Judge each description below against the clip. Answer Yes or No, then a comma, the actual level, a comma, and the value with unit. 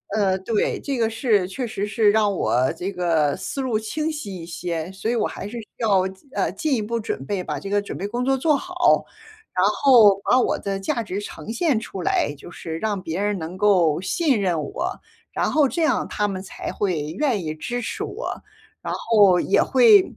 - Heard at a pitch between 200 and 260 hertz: Yes, high, 205 Hz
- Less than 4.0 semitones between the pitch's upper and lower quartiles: No, average, 4.6 semitones